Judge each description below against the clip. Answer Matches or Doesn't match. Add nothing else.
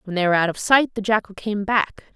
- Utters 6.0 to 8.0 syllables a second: Matches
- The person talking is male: Doesn't match